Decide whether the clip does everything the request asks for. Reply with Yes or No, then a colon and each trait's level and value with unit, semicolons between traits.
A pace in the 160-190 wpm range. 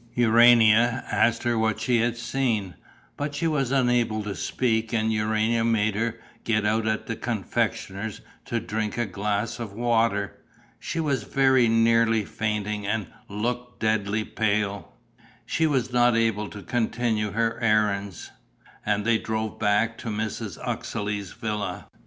No: average, 145 wpm